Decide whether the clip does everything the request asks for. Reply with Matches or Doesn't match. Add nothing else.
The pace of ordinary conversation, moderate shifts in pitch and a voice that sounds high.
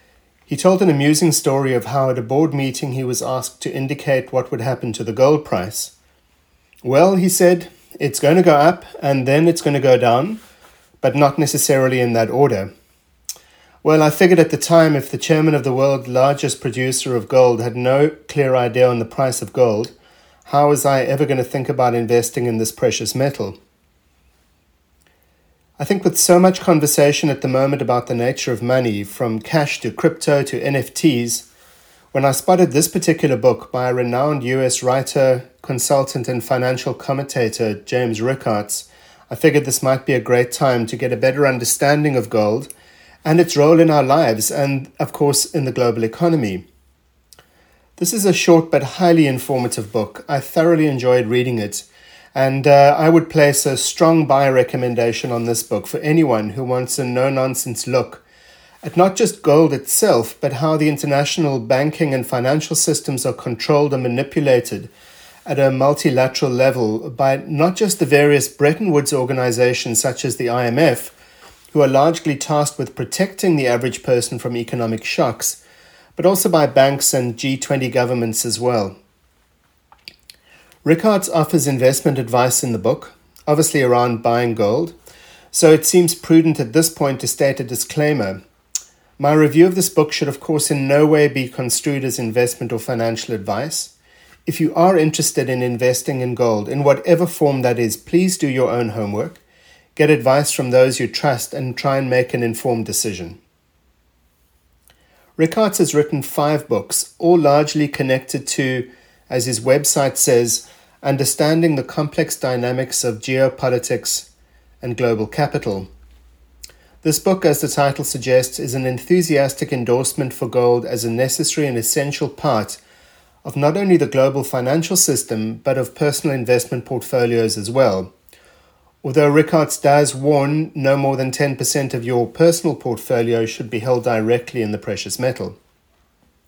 Doesn't match